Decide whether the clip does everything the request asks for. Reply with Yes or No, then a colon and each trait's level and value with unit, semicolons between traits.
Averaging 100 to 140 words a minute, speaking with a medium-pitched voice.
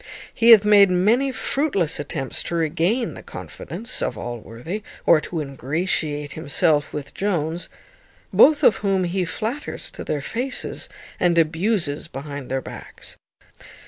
Yes: slow, 135 wpm; medium, 170 Hz